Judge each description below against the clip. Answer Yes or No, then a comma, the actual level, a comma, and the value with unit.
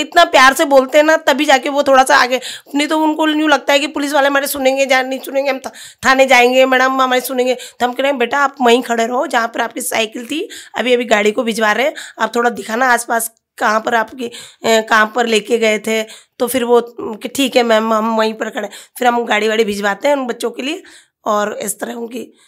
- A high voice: Yes, very high, 250 Hz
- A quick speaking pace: Yes, fast, 250 wpm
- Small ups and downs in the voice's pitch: No, average, 3.3 semitones